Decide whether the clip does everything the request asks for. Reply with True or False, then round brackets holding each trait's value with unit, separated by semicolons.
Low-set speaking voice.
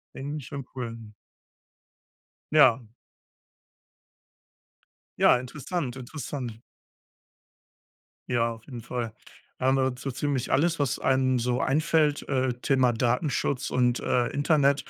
True (130 Hz)